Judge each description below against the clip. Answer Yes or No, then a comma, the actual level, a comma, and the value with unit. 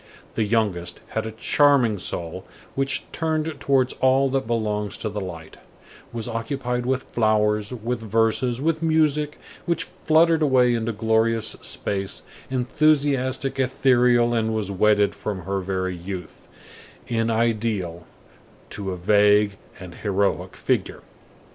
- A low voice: Yes, low, 115 Hz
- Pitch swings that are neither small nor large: Yes, average, 4.3 semitones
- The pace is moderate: No, slow, 130 wpm